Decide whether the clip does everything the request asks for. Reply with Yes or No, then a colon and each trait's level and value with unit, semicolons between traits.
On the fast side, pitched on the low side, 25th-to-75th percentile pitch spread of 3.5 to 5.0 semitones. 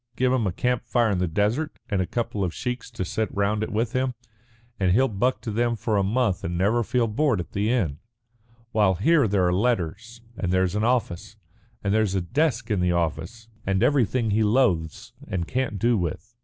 Yes: fast, 210 wpm; low, 110 Hz; average, 4.5 semitones